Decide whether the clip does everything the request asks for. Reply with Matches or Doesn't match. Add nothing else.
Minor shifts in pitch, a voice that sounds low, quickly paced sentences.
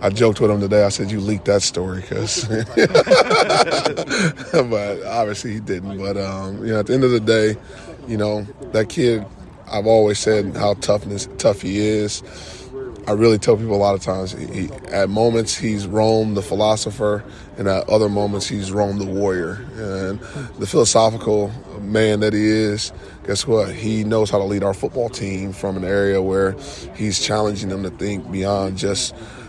Doesn't match